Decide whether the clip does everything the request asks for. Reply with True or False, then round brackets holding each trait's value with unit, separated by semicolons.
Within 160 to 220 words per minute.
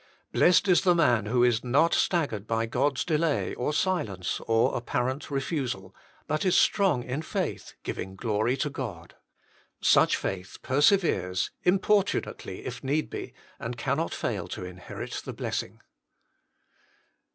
False (140 wpm)